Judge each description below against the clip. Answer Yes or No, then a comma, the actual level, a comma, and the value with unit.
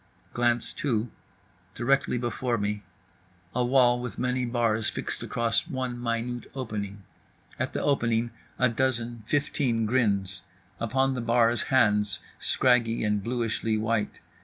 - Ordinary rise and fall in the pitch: No, narrow, 2.1 semitones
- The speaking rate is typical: No, slow, 125 wpm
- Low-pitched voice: Yes, low, 120 Hz